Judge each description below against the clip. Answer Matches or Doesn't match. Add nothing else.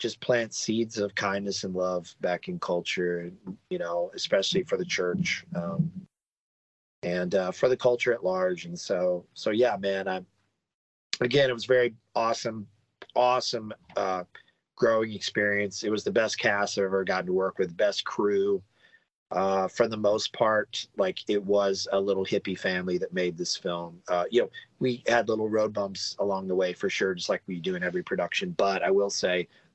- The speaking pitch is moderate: Doesn't match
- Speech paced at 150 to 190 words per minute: Matches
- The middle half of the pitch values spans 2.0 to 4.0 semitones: Doesn't match